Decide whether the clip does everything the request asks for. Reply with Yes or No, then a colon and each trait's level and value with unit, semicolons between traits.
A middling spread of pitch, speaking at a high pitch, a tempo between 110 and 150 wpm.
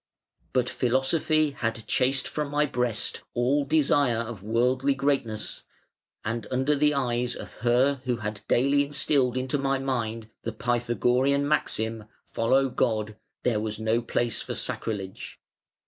No: average, 3.3 semitones; low, 125 Hz; slow, 135 wpm